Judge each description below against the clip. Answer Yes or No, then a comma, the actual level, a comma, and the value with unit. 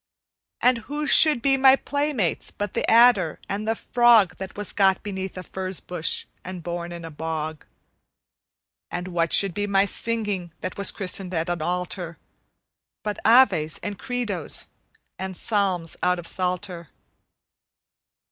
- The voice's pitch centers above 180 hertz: Yes, high, 190 Hz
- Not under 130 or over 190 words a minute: Yes, average, 145 wpm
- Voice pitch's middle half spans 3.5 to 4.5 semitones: Yes, average, 3.9 semitones